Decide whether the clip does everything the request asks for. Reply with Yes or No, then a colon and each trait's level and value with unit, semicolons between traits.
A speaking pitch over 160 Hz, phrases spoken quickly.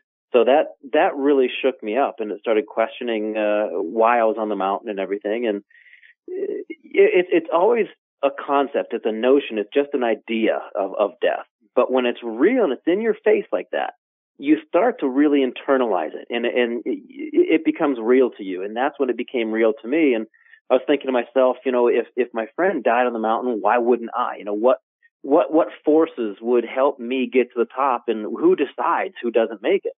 No: low, 130 Hz; fast, 220 wpm